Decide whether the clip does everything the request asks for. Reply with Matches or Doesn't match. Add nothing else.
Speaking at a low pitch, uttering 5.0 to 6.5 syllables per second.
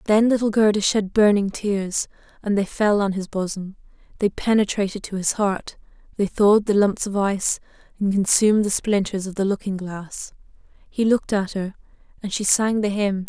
Doesn't match